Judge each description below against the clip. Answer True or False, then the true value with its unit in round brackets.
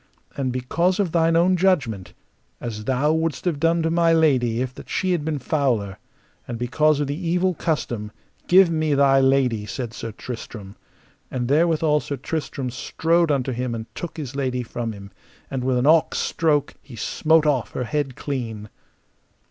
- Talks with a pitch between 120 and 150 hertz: True (140 Hz)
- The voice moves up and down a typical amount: True (4.8 semitones)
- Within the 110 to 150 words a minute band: False (175 wpm)